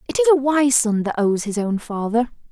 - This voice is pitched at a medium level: No, high, 245 Hz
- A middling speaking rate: No, fast, 240 wpm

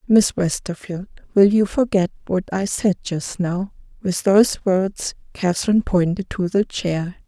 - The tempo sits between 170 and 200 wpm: No, average, 150 wpm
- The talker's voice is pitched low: No, high, 190 Hz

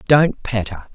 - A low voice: Yes, low, 125 Hz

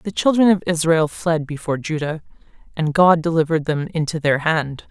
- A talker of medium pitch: Yes, medium, 160 Hz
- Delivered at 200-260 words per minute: No, average, 170 wpm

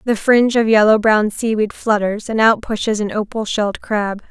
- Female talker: Yes, female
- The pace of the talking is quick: No, average, 195 wpm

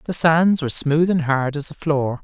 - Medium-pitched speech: Yes, medium, 155 Hz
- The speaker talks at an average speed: No, fast, 240 wpm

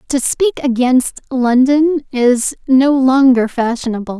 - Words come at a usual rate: No, slow, 115 wpm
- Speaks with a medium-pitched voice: No, very high, 260 Hz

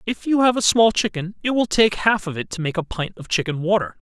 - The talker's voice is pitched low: No, high, 190 Hz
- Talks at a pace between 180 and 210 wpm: No, fast, 280 wpm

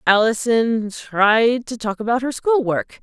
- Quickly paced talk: No, average, 160 wpm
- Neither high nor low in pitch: No, high, 225 Hz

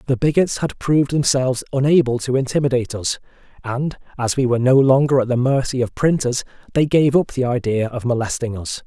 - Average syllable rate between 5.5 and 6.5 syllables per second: Yes, 5.9 syllables/s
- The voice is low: Yes, low, 130 Hz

